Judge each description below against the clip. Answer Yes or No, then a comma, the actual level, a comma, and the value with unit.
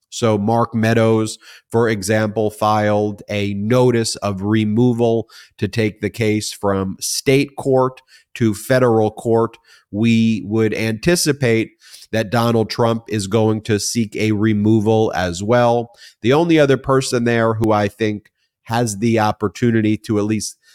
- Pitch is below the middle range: Yes, low, 110 Hz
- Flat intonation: Yes, narrow, 1.7 semitones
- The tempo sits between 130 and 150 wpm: Yes, average, 140 wpm